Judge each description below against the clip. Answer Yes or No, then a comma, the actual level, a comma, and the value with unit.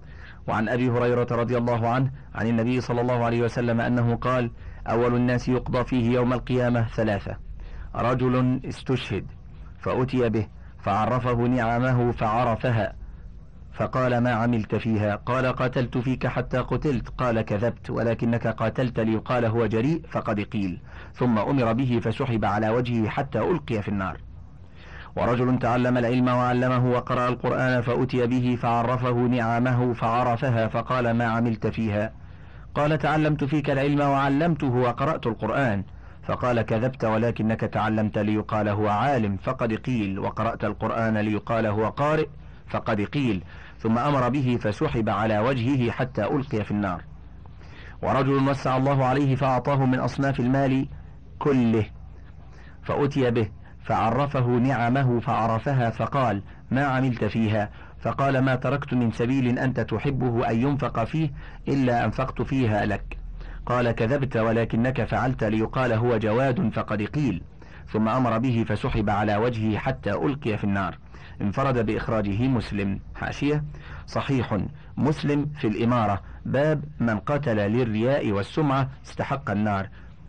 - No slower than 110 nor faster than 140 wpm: Yes, average, 125 wpm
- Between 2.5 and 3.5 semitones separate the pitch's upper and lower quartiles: Yes, average, 2.9 semitones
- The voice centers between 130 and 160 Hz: No, low, 120 Hz